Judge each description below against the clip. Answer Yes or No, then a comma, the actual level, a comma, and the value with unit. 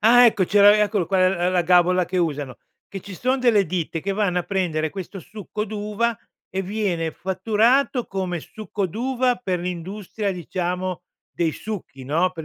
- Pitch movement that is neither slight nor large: Yes, average, 3.2 semitones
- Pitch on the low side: No, high, 190 Hz